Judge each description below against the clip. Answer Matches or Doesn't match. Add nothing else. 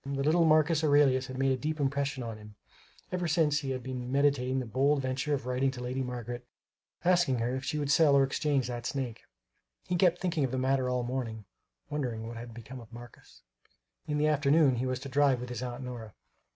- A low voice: Matches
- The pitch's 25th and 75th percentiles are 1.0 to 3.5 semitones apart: Matches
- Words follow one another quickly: Matches